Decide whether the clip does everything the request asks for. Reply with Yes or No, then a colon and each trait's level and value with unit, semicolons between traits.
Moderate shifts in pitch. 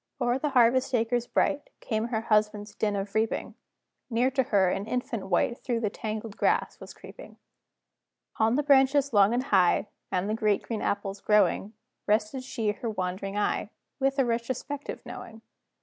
Yes: average, 3.3 semitones